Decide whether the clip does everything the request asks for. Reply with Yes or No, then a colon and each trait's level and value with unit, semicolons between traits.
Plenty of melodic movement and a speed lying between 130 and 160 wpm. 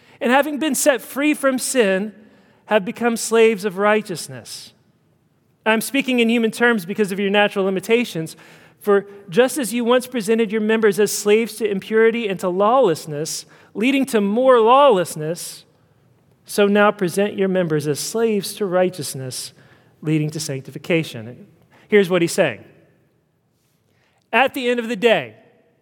Yes: wide, 6.3 semitones; average, 145 wpm